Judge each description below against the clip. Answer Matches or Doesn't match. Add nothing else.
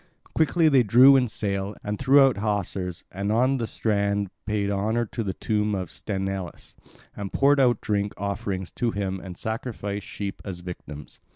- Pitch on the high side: Doesn't match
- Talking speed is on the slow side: Doesn't match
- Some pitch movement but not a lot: Matches